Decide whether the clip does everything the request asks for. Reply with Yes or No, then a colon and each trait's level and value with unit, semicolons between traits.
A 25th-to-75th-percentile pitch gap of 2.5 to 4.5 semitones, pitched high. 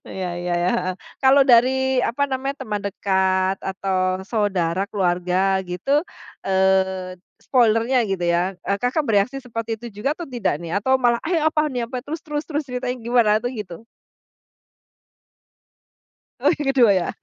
No: wide, 5.5 semitones; high, 220 Hz